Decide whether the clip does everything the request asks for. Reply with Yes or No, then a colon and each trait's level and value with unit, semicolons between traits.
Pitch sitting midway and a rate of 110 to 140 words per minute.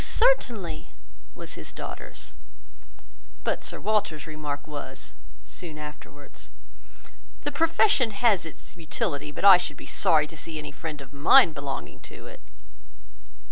Yes: medium, 155 Hz; slow, 135 wpm